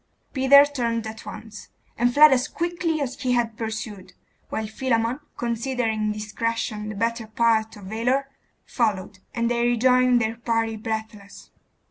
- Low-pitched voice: No, high, 230 Hz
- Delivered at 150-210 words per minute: No, average, 140 wpm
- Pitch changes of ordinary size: No, narrow, 2.3 semitones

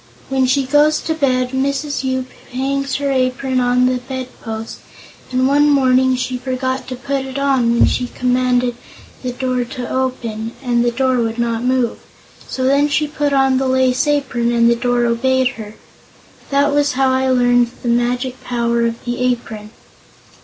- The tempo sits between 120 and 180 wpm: Yes, average, 175 wpm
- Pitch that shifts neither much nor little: No, narrow, 1.7 semitones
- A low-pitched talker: No, very high, 255 Hz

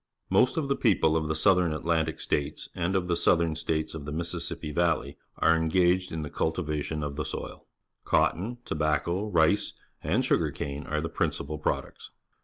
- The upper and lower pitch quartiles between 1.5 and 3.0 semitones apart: Yes, narrow, 2.4 semitones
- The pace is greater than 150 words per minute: Yes, average, 175 wpm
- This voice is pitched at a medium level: No, very low, 80 Hz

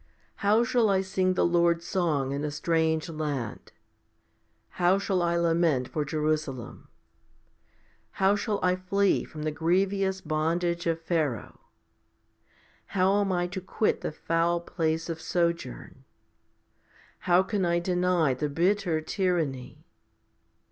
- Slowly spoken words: Yes, slow, 130 wpm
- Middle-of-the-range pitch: Yes, medium, 170 Hz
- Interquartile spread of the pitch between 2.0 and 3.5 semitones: Yes, average, 3.2 semitones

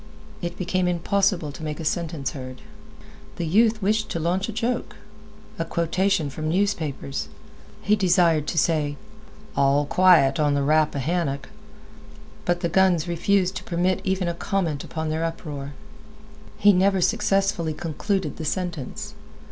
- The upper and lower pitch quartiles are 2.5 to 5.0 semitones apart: Yes, average, 3.9 semitones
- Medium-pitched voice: Yes, medium, 170 Hz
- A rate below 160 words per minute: Yes, average, 140 wpm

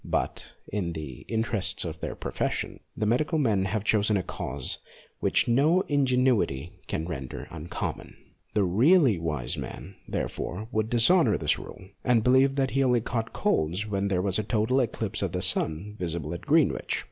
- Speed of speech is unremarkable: Yes, average, 170 wpm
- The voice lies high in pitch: No, low, 105 Hz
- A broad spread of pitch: Yes, wide, 6.2 semitones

